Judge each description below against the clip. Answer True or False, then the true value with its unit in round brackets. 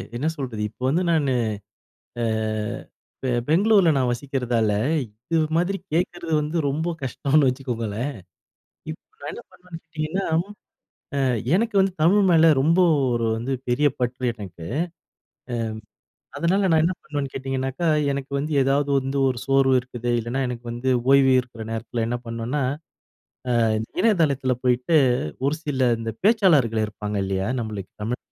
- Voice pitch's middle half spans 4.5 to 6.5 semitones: True (4.9 semitones)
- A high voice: False (135 Hz)